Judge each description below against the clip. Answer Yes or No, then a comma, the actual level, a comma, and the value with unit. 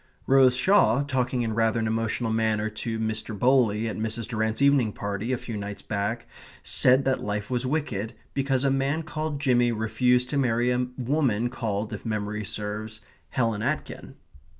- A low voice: Yes, low, 115 Hz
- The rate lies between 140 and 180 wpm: Yes, average, 170 wpm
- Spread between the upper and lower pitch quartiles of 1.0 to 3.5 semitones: Yes, average, 3.1 semitones